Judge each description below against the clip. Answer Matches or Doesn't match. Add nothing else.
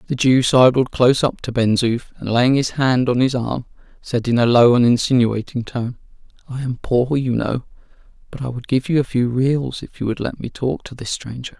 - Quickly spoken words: Matches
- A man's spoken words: Matches